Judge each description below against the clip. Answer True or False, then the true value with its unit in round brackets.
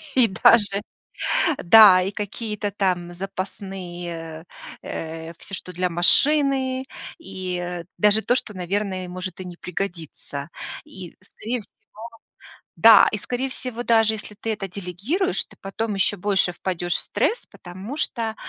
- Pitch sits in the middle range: False (195 Hz)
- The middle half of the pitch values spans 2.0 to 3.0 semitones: False (3.7 semitones)